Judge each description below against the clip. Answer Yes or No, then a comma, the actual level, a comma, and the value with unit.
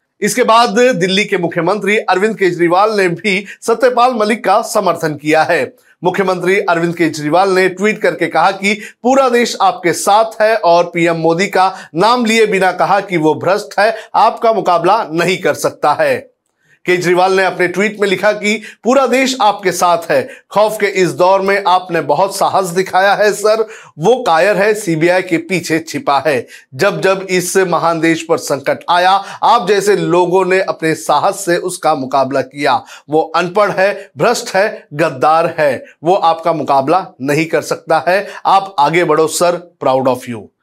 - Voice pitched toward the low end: No, medium, 185 Hz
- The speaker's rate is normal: Yes, average, 170 wpm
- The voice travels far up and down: No, average, 3.8 semitones